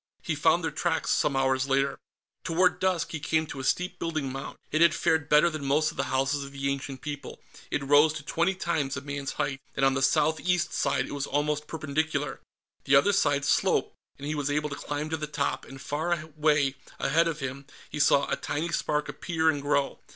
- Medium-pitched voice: Yes, medium, 150 Hz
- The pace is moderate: No, fast, 220 wpm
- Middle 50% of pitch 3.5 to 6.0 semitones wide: No, narrow, 2.4 semitones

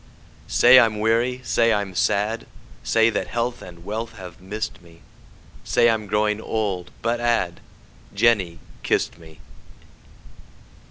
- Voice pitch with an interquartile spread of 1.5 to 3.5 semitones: No, average, 4.0 semitones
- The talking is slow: Yes, slow, 130 wpm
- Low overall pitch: Yes, low, 105 Hz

